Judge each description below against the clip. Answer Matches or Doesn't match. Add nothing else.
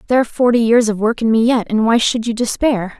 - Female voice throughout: Matches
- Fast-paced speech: Matches